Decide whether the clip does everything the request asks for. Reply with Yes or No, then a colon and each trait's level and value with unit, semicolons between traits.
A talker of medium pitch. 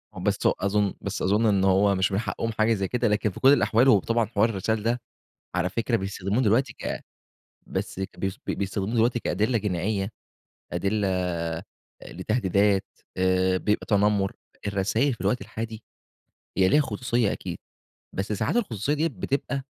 No: low, 105 Hz